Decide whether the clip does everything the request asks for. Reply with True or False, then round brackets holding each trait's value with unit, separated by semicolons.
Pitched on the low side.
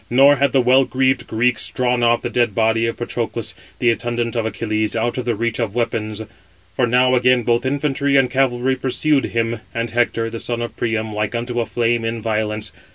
True (120 Hz)